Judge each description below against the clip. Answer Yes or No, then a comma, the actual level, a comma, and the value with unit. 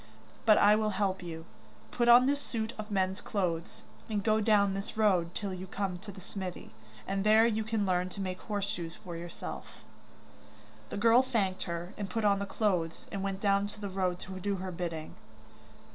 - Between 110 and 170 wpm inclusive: No, average, 195 wpm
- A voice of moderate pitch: No, high, 195 Hz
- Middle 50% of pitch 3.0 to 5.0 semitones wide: No, narrow, 2.6 semitones